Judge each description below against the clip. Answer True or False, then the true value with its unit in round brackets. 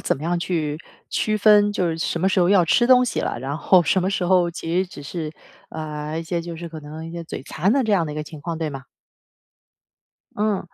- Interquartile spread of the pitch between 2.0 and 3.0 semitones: False (3.4 semitones)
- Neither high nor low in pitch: True (170 Hz)